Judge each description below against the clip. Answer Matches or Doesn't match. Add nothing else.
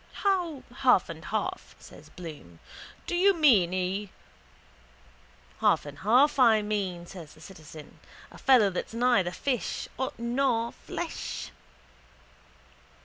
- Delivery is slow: Matches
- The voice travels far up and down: Matches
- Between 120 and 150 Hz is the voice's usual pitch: Doesn't match